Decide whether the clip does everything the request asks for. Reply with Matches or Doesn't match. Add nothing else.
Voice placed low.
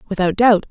Doesn't match